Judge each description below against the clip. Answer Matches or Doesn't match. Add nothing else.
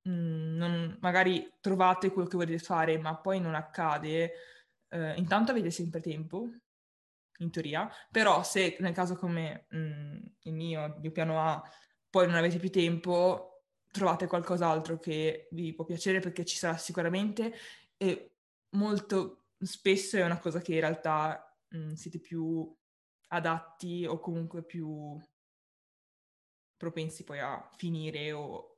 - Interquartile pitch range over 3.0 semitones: Doesn't match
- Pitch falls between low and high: Matches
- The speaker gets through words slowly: Doesn't match